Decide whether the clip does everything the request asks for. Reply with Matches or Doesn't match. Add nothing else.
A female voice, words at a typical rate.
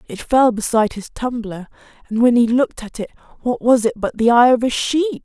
Doesn't match